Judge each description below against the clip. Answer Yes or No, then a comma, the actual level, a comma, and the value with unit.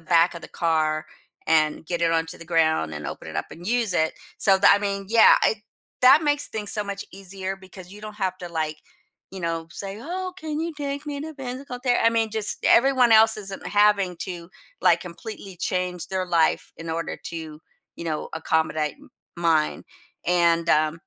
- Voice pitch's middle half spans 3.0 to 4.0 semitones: No, average, 5.0 semitones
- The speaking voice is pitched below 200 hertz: Yes, medium, 185 Hz